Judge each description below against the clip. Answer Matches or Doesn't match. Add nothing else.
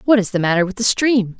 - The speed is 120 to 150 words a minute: Doesn't match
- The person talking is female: Matches